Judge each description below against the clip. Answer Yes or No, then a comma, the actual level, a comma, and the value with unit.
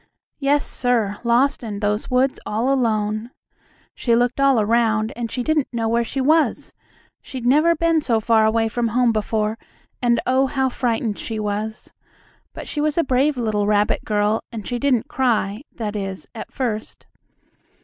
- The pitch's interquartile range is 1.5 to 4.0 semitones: Yes, average, 3.3 semitones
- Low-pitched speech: No, high, 235 Hz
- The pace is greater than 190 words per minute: No, average, 170 wpm